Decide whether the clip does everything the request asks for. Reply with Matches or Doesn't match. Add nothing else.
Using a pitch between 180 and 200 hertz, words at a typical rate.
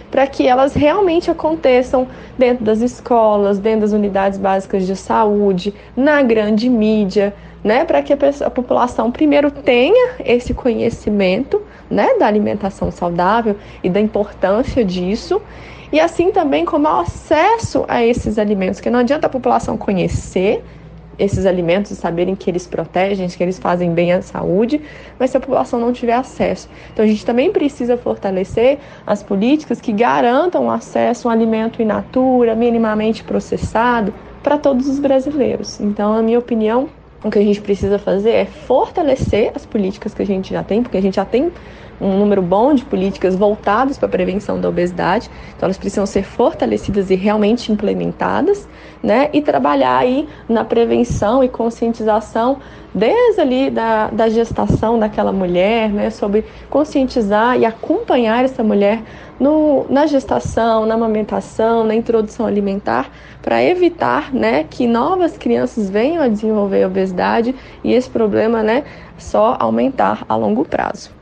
Doesn't match